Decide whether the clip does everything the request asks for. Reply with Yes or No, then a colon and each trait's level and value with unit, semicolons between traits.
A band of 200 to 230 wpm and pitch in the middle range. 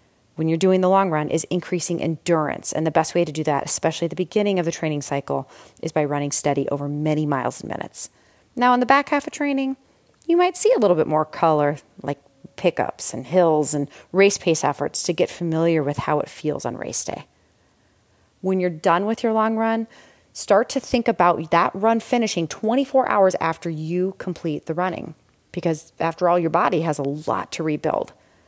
Yes: fast, 205 wpm; medium, 170 Hz